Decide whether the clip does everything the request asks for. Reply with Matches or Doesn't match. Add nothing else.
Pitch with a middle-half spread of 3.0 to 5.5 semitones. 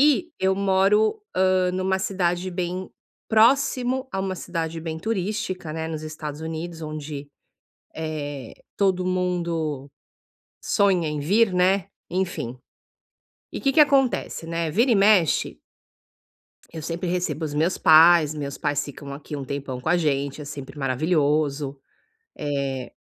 Matches